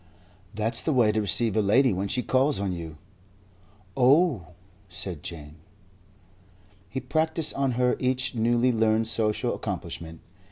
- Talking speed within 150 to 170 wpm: No, slow, 135 wpm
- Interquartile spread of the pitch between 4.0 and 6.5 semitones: Yes, average, 4.7 semitones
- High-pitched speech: No, low, 115 Hz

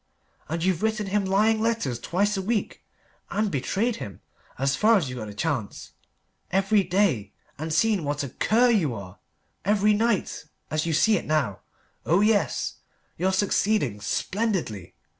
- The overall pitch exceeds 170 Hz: Yes, high, 190 Hz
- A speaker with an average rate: Yes, average, 160 wpm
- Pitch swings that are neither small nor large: No, wide, 6.8 semitones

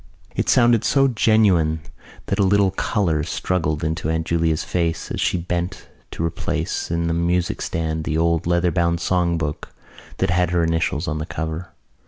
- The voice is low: Yes, very low, 85 Hz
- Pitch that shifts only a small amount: Yes, narrow, 2.1 semitones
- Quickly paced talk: No, average, 170 wpm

